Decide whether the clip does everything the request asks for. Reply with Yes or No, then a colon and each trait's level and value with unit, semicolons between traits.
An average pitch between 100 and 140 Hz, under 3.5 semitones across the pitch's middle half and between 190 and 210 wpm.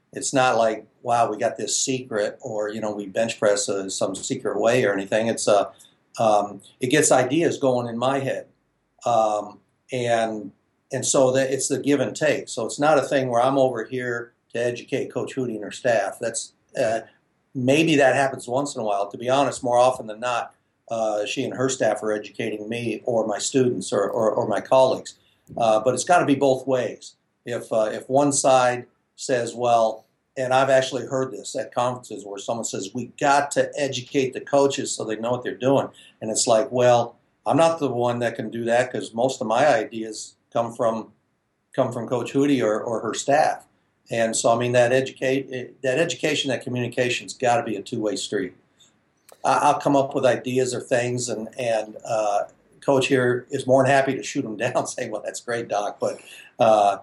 Yes: low, 125 Hz; average, 3.0 semitones; fast, 205 wpm